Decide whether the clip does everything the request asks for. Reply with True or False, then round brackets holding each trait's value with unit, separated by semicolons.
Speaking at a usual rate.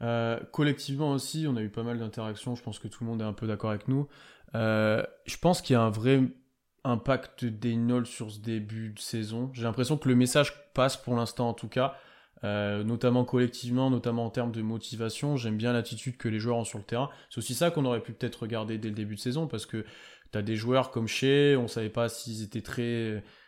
False (240 wpm)